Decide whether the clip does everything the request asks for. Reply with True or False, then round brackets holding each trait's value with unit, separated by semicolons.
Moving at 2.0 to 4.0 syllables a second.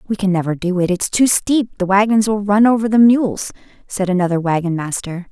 False (5.4 syllables/s)